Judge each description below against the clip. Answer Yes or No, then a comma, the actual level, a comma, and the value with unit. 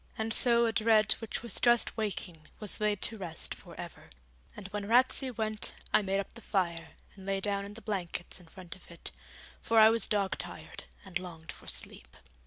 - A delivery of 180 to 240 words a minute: Yes, average, 200 wpm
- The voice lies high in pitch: Yes, high, 205 Hz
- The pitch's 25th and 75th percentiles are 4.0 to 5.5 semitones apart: No, average, 3.1 semitones